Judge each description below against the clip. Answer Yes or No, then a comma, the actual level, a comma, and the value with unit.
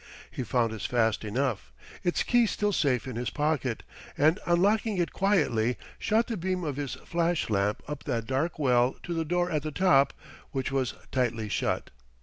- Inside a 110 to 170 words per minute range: No, average, 180 wpm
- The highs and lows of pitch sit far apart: Yes, wide, 6.1 semitones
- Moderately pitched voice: Yes, medium, 145 Hz